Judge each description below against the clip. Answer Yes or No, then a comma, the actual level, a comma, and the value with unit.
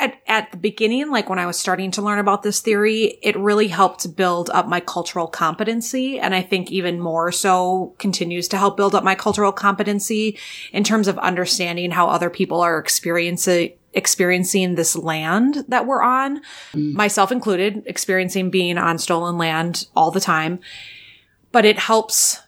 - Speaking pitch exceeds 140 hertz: Yes, high, 190 Hz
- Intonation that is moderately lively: Yes, average, 3.2 semitones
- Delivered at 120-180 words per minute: Yes, average, 170 wpm